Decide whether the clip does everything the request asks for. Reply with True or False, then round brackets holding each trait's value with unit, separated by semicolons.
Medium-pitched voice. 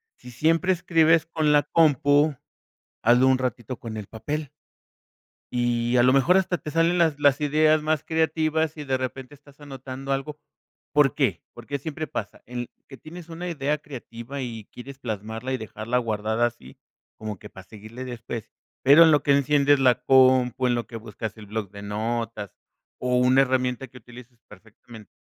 False (130 Hz)